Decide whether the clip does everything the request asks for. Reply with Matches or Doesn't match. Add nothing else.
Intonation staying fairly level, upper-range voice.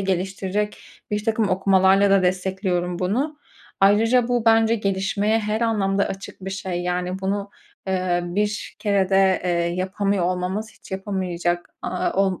Matches